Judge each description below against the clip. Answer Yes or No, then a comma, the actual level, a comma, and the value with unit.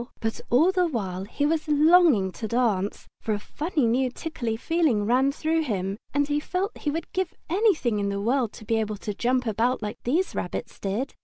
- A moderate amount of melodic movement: No, wide, 6.6 semitones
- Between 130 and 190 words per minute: No, fast, 205 wpm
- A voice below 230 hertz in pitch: No, very high, 250 Hz